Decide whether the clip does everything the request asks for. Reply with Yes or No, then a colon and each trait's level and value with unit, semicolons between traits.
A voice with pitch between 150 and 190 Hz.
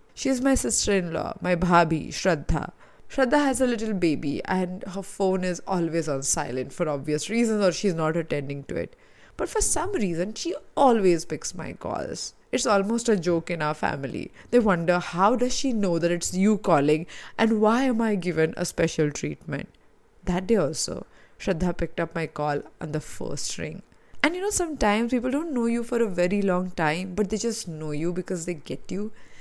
Yes: medium, 185 Hz